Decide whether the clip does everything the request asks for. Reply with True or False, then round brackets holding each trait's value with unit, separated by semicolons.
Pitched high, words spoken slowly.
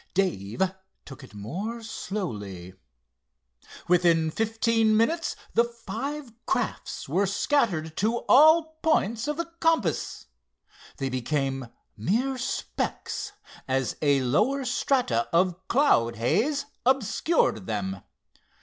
True (200 Hz; 105 wpm)